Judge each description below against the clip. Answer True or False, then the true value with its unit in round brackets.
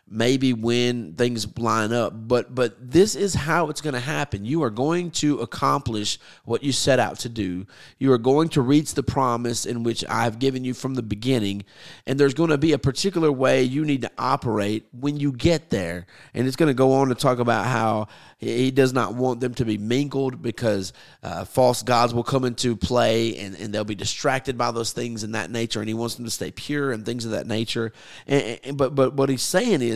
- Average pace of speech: False (230 wpm)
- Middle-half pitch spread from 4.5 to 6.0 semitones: False (3.2 semitones)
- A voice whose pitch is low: True (125 Hz)